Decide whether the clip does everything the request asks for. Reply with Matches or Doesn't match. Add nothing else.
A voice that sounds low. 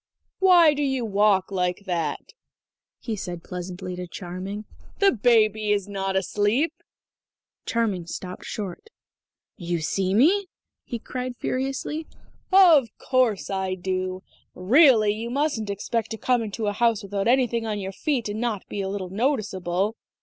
Doesn't match